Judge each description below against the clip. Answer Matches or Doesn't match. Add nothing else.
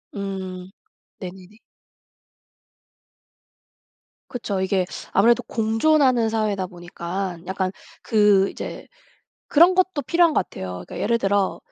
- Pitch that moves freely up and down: Doesn't match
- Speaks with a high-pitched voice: Matches